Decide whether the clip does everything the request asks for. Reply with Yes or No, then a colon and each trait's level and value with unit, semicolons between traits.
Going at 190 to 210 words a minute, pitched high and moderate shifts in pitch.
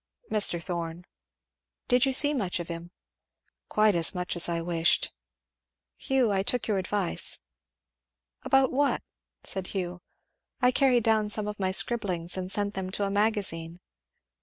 No: average, 150 wpm; high, 195 Hz; average, 4.0 semitones